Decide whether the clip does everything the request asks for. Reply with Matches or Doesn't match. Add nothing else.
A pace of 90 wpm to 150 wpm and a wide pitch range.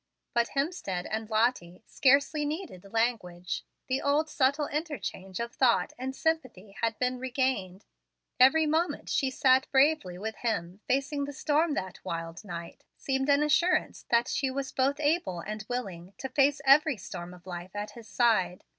Doesn't match